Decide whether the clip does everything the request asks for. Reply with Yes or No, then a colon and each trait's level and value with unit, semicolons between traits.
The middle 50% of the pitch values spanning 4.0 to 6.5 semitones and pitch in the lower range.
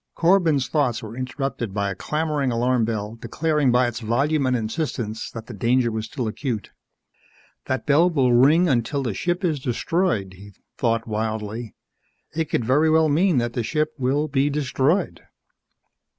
Yes: average, 5.0 semitones; low, 130 Hz